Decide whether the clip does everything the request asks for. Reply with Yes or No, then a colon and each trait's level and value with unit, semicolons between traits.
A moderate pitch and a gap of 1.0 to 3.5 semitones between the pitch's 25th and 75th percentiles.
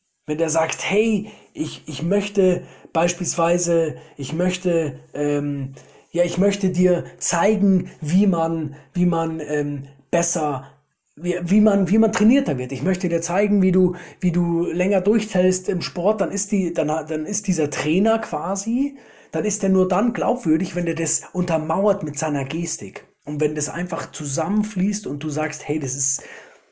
No: medium, 175 Hz; average, 4.0 semitones